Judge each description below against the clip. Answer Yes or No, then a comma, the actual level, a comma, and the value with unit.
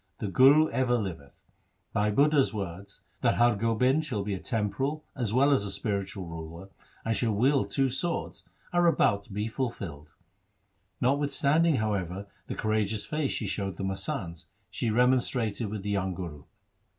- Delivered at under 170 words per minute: Yes, average, 155 wpm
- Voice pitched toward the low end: Yes, low, 110 Hz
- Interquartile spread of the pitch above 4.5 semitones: Yes, average, 5.1 semitones